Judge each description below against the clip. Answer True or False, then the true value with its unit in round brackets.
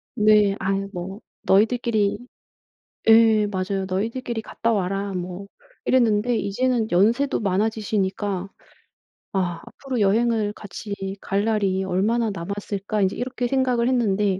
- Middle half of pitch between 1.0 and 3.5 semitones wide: True (2.9 semitones)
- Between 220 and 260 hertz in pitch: False (205 Hz)